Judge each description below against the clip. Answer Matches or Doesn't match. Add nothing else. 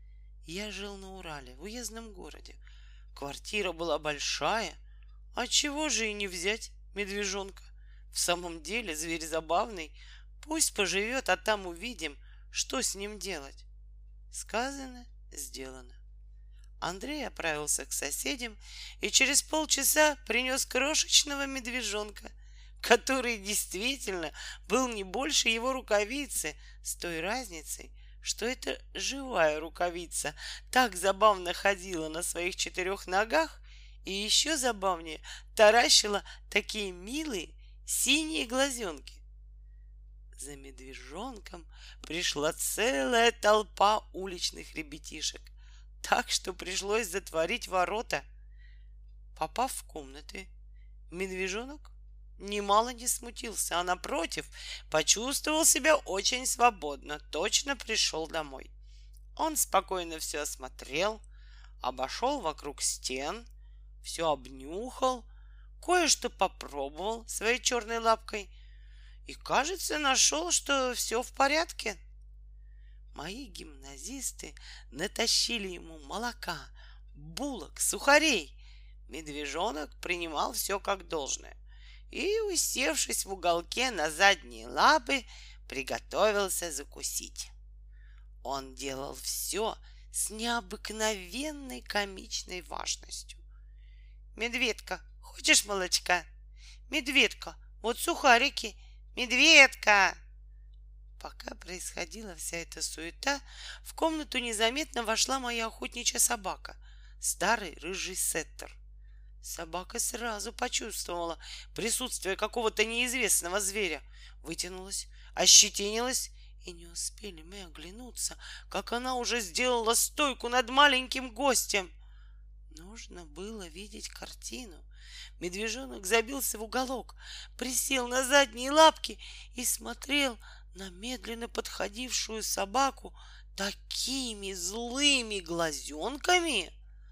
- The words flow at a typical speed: Doesn't match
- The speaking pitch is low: Doesn't match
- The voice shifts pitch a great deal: Matches